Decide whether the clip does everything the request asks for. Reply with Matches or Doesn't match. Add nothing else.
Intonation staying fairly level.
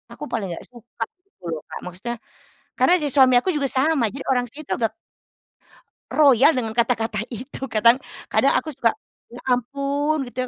Doesn't match